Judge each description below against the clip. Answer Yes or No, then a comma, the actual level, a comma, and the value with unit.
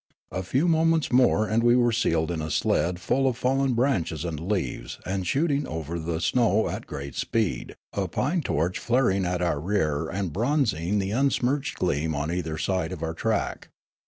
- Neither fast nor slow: Yes, average, 185 wpm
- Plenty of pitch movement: Yes, wide, 7.1 semitones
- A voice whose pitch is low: Yes, very low, 95 Hz